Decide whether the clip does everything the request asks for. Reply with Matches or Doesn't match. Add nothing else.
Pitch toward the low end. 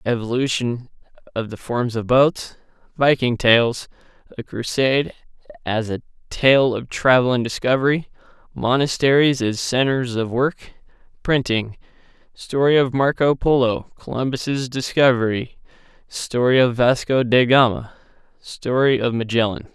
Matches